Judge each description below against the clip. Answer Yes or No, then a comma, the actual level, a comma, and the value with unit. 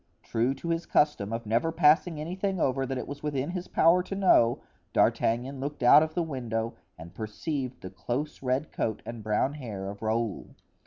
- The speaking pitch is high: No, low, 135 Hz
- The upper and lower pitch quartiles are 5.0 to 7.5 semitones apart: Yes, wide, 5.4 semitones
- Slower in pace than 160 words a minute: No, average, 190 wpm